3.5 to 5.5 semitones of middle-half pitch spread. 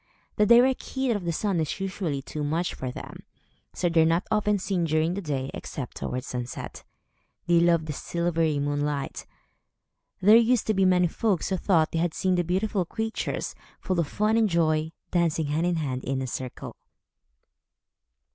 Yes: average, 4.0 semitones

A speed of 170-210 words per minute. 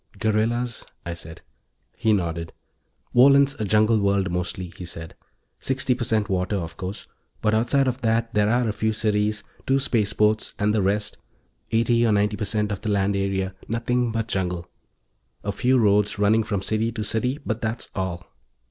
Yes: average, 175 wpm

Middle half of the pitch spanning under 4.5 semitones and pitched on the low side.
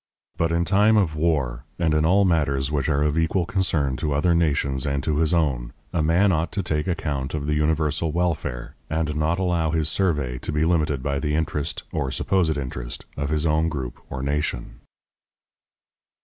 Yes: average, 2.8 semitones; very low, 75 Hz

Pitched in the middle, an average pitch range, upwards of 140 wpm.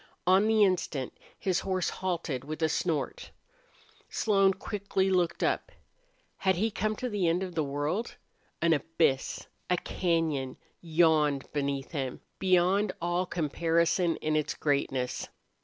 No: medium, 170 Hz; average, 3.9 semitones; slow, 135 wpm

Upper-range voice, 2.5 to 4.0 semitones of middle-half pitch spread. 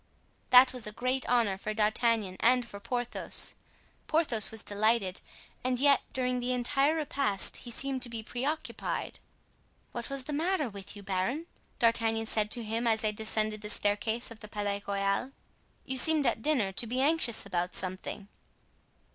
Yes: high, 230 Hz; average, 3.5 semitones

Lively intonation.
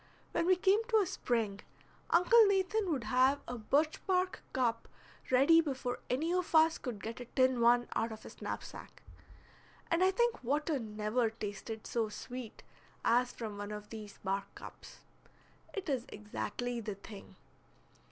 Yes: wide, 7.0 semitones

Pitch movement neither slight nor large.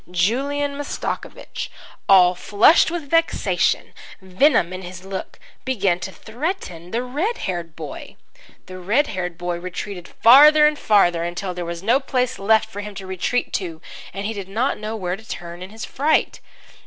No: wide, 6.3 semitones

